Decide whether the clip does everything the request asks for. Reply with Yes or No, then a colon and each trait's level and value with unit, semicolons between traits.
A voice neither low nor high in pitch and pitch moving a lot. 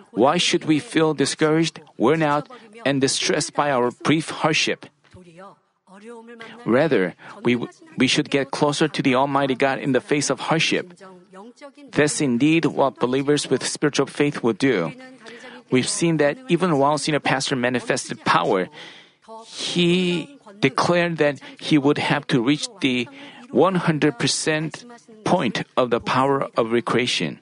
No: medium, 150 Hz; average, 4.7 semitones